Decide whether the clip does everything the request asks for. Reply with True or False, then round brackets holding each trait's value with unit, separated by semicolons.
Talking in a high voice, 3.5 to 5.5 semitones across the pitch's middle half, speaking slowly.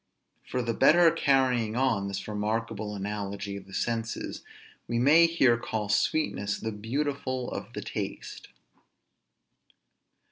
False (115 Hz; 4.2 semitones; 120 wpm)